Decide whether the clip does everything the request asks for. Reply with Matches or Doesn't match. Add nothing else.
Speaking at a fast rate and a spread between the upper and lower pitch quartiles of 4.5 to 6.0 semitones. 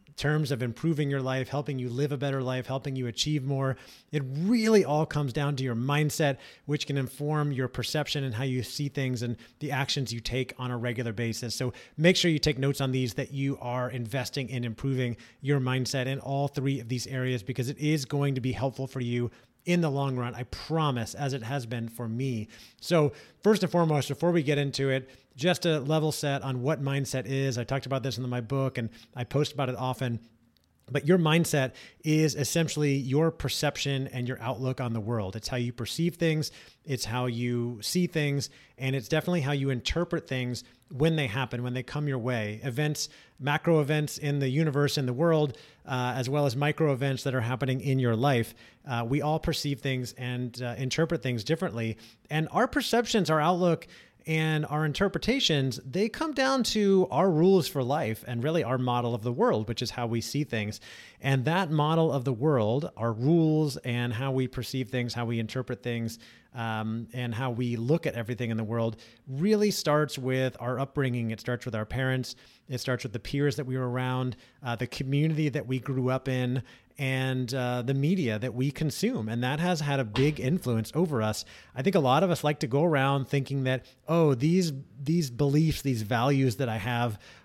Doesn't match